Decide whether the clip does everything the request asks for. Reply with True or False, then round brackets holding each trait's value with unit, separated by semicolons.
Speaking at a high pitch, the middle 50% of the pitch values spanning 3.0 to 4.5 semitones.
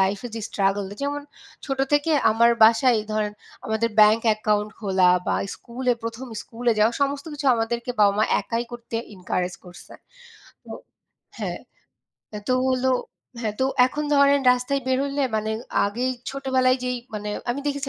True (235 Hz; 3.8 semitones)